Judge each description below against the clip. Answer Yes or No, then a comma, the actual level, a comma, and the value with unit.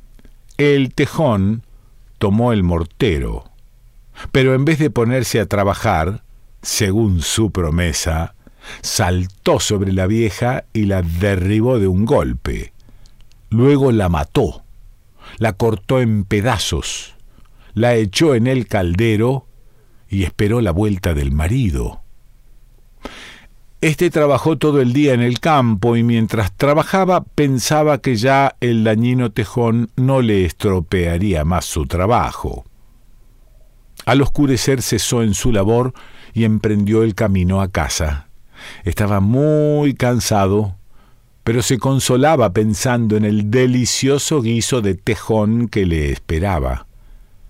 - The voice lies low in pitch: Yes, low, 115 Hz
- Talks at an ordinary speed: No, slow, 120 wpm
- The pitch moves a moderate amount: Yes, average, 4.0 semitones